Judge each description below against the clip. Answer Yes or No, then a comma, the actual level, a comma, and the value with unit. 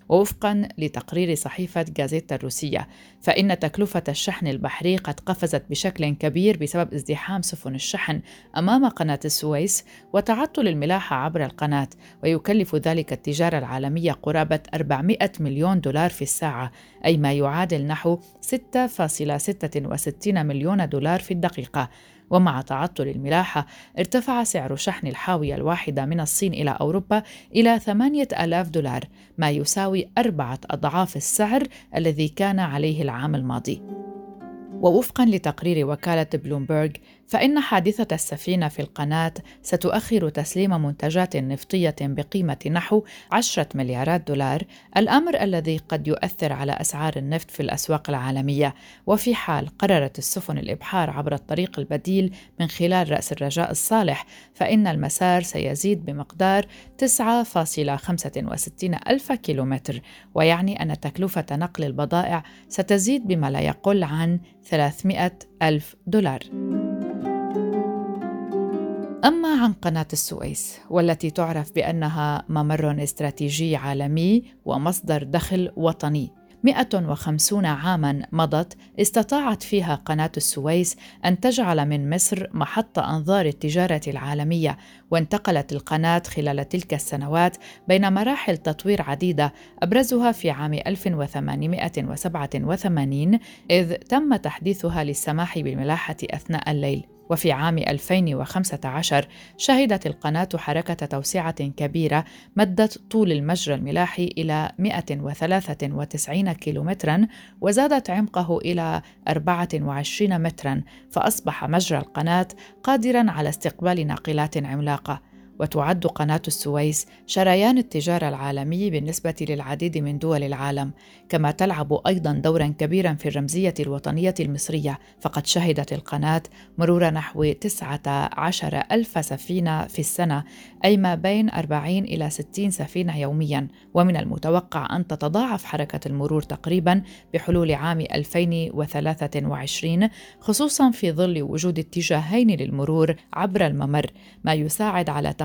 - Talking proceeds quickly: No, average, 110 wpm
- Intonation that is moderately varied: Yes, average, 4.3 semitones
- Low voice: No, medium, 165 Hz